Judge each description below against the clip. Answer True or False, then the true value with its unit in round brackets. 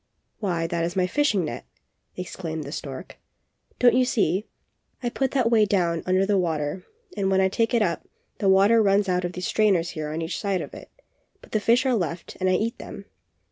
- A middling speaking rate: False (215 wpm)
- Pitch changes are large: False (4.1 semitones)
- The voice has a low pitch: False (190 Hz)